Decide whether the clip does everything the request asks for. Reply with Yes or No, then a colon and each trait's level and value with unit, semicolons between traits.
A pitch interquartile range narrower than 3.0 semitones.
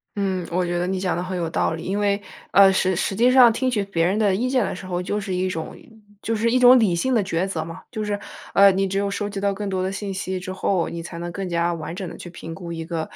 Yes: narrow, 2.6 semitones